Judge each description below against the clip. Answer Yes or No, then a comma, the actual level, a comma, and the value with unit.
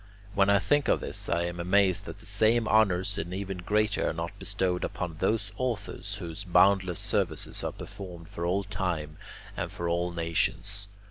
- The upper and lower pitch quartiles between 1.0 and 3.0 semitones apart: Yes, average, 2.7 semitones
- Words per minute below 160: No, average, 180 wpm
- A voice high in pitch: No, very low, 95 Hz